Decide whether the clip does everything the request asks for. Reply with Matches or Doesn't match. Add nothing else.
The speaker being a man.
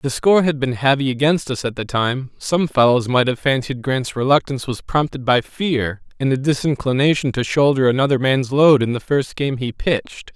Matches